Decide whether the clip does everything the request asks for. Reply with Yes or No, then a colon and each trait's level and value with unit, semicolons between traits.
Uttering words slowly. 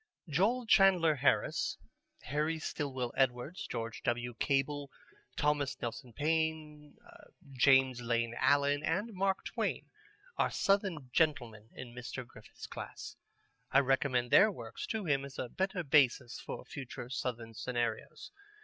Yes: slow, 125 wpm